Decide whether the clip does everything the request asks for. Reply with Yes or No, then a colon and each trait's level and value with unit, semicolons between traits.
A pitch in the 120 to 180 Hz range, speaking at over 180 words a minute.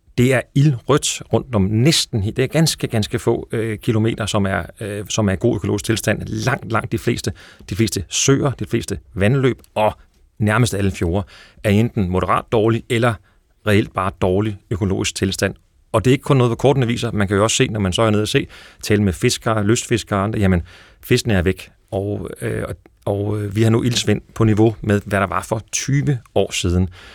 No: low, 110 Hz; average, 210 wpm